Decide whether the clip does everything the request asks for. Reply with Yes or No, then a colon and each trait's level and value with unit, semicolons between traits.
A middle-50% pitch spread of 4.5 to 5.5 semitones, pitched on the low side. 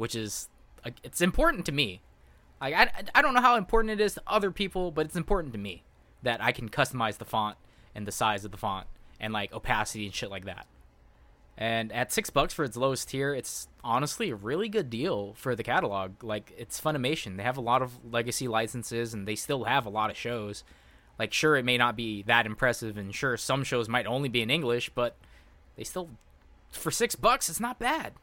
Yes: average, 5.1 semitones; low, 120 Hz